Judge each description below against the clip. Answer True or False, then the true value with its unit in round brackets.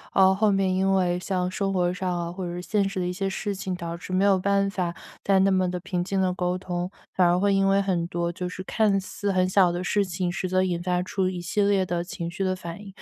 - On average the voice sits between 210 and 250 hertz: False (185 Hz)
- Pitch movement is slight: True (1.6 semitones)